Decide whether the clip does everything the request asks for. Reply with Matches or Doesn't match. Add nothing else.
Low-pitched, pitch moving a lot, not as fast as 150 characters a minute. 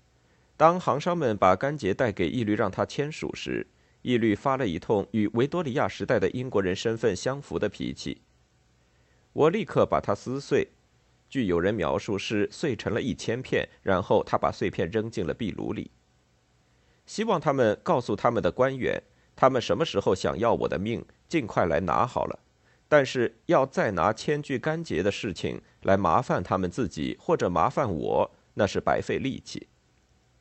Doesn't match